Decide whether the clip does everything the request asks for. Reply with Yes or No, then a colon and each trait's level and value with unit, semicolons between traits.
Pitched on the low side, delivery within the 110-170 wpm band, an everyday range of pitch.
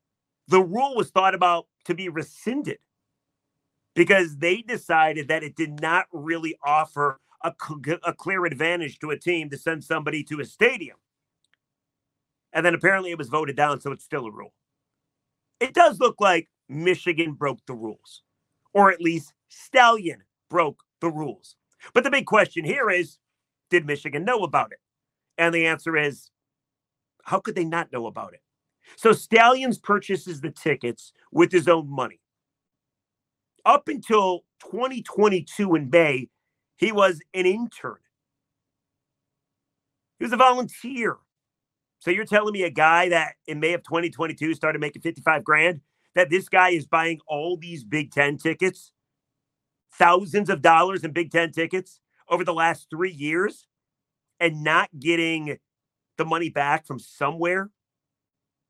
No: medium, 165 Hz; average, 150 wpm; average, 4.0 semitones